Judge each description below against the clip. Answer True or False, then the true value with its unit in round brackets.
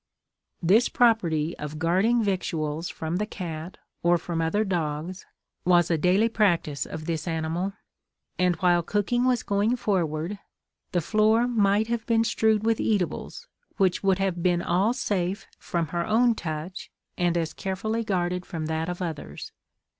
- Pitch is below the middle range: False (180 Hz)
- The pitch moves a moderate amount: True (4.2 semitones)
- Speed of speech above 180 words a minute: False (155 wpm)